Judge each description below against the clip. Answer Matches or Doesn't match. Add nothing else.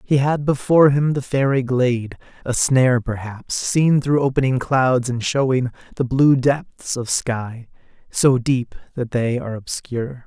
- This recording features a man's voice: Matches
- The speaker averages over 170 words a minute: Doesn't match